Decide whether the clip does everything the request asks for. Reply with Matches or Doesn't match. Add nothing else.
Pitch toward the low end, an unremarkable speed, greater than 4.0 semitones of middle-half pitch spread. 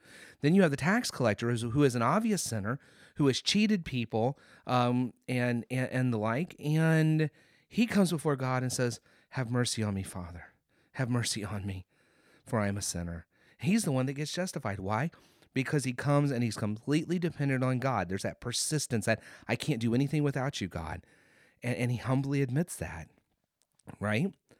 Matches